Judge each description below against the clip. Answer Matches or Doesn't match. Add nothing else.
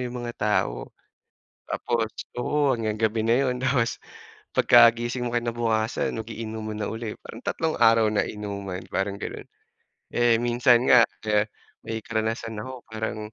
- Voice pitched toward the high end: Doesn't match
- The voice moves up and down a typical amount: Doesn't match